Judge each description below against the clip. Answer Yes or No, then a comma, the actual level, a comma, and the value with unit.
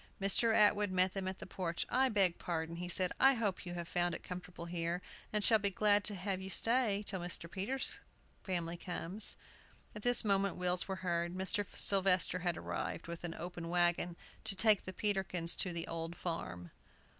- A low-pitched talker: No, medium, 185 Hz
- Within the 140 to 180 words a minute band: No, average, 190 wpm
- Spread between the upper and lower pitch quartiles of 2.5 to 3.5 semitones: Yes, average, 2.8 semitones